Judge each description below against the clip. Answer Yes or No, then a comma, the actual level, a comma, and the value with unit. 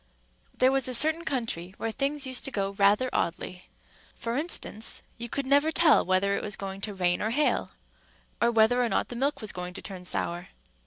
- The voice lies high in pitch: Yes, high, 230 Hz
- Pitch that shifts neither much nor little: No, wide, 5.7 semitones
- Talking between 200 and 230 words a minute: Yes, fast, 205 wpm